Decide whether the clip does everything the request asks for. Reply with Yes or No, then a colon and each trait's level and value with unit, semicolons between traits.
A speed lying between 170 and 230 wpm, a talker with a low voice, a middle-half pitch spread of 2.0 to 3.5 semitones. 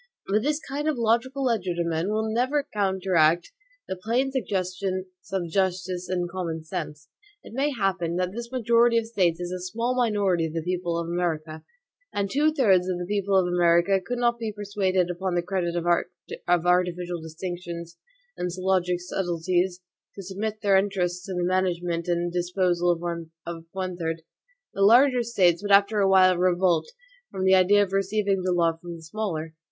No: average, 175 wpm; medium, 185 Hz; average, 2.8 semitones